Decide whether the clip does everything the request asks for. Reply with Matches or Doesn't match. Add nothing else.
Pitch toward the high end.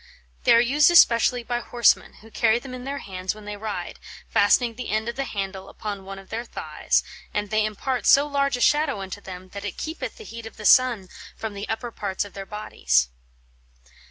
Matches